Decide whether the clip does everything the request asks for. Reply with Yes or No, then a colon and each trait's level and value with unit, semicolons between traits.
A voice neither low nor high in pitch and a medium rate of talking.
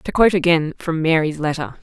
Yes: medium, 165 Hz; average, 195 wpm